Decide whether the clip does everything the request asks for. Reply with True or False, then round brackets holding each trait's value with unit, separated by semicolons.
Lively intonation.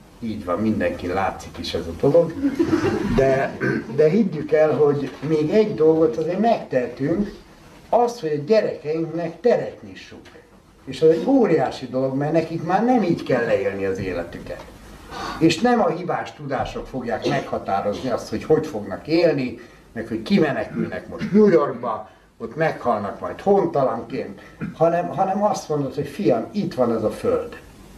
True (6.7 semitones)